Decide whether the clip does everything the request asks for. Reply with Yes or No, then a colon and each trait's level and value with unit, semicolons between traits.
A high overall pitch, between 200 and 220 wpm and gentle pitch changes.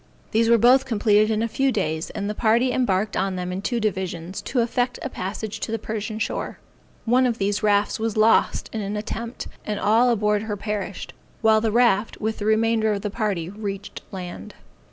Yes: high, 215 Hz; fast, 205 wpm; narrow, 2.1 semitones